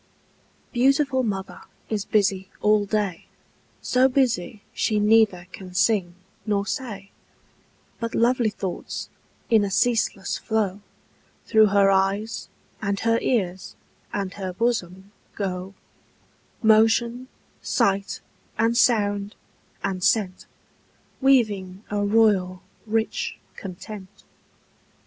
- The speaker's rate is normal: No, slow, 105 wpm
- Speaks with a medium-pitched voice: No, high, 205 Hz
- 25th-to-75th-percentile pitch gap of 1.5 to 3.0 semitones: Yes, average, 2.7 semitones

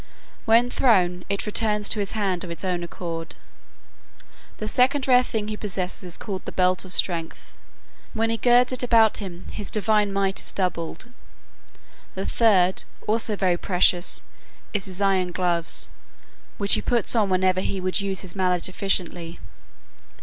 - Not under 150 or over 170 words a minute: Yes, average, 160 wpm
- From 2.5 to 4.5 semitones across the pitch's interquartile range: Yes, average, 3.1 semitones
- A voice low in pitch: No, high, 195 Hz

